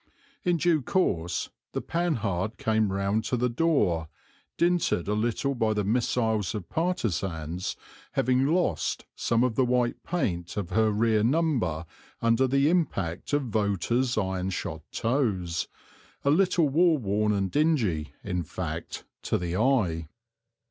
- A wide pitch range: Yes, wide, 6.4 semitones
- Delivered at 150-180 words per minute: No, average, 140 wpm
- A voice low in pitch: Yes, low, 110 Hz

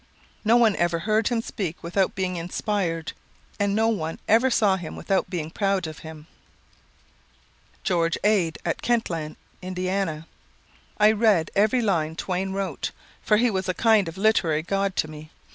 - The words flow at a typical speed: Yes, average, 160 wpm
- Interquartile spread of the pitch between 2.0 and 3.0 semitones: No, average, 4.3 semitones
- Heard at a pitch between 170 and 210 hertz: Yes, high, 190 Hz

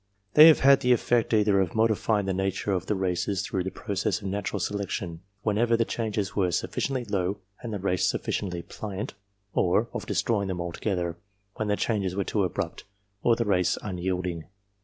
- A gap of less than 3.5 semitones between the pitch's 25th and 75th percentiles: Yes, average, 3.0 semitones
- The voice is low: Yes, low, 100 Hz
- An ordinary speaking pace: Yes, average, 190 wpm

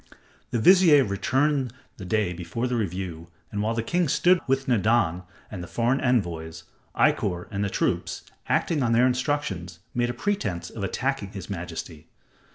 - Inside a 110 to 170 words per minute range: Yes, average, 165 wpm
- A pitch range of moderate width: No, wide, 6.5 semitones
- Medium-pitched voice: No, low, 110 Hz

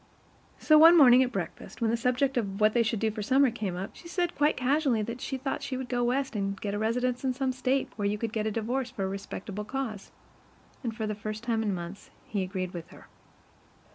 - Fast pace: Yes, fast, 245 wpm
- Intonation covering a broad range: No, average, 3.8 semitones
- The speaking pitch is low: No, high, 230 Hz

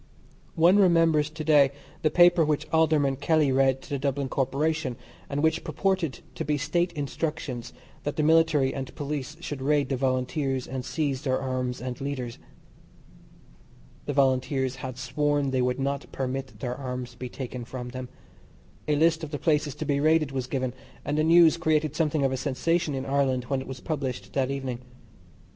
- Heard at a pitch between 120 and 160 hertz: Yes, medium, 140 Hz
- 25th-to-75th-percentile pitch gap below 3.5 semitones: Yes, average, 3.0 semitones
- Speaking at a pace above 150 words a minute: Yes, average, 180 wpm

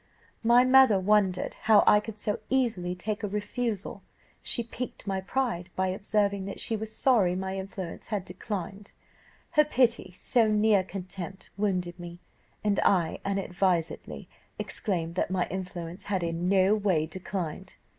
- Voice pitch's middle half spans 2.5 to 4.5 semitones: Yes, average, 2.8 semitones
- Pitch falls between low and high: No, high, 195 Hz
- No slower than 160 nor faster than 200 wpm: No, average, 145 wpm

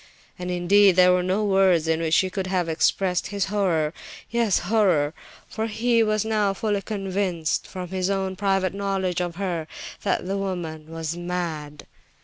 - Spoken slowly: No, average, 165 wpm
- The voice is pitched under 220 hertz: Yes, medium, 185 Hz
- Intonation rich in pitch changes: No, narrow, 2.4 semitones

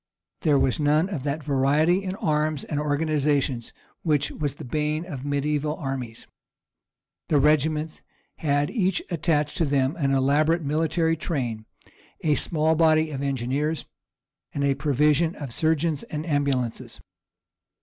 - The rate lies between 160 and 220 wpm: No, slow, 135 wpm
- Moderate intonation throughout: No, narrow, 2.2 semitones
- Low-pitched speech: No, medium, 150 Hz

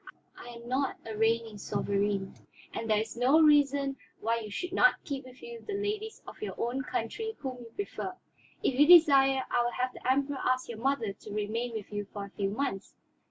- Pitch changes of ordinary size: Yes, average, 4.3 semitones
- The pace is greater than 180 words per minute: Yes, fast, 205 wpm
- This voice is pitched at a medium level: No, very high, 250 Hz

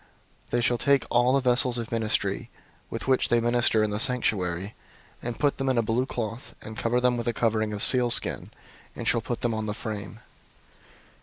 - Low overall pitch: Yes, low, 120 Hz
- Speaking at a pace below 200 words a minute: No, fast, 205 wpm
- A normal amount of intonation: No, narrow, 2.2 semitones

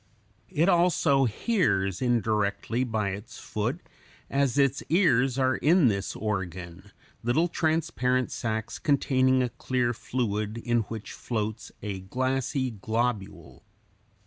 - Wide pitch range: No, average, 4.3 semitones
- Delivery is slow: Yes, slow, 115 wpm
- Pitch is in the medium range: No, low, 120 Hz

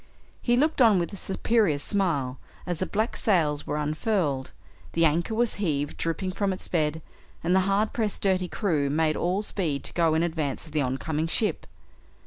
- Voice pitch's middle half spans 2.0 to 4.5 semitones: No, average, 4.9 semitones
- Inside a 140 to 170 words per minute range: No, average, 185 wpm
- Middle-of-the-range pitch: Yes, medium, 170 Hz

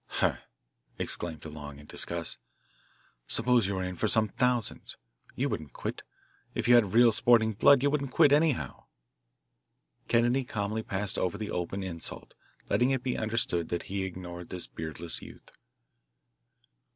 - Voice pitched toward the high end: No, low, 105 Hz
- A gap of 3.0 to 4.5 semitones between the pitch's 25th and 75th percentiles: No, wide, 5.6 semitones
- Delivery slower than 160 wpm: Yes, average, 150 wpm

